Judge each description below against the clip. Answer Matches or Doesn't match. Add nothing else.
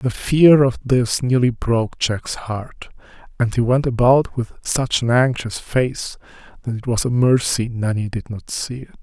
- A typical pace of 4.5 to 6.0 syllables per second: Doesn't match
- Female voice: Doesn't match